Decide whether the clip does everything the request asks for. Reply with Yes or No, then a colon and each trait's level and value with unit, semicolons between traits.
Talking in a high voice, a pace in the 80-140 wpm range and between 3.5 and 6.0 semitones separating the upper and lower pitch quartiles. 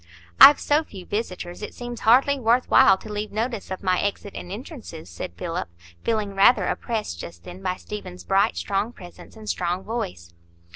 No: high, 200 Hz; average, 180 wpm; average, 4.1 semitones